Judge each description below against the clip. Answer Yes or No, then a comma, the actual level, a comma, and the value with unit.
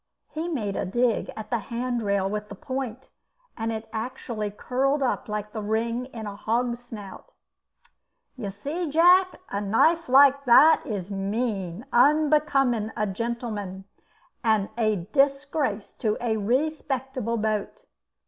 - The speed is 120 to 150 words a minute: Yes, average, 140 wpm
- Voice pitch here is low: No, high, 235 Hz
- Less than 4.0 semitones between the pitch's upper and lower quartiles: No, average, 4.4 semitones